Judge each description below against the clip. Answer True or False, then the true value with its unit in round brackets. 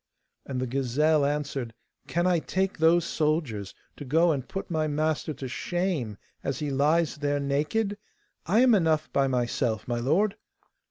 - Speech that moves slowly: False (160 wpm)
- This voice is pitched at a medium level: True (150 Hz)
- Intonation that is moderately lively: True (4.0 semitones)